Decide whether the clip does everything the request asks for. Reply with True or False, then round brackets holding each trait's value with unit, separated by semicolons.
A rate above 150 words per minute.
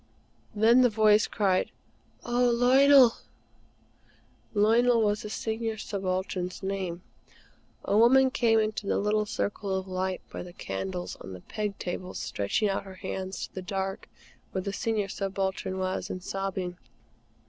False (145 wpm)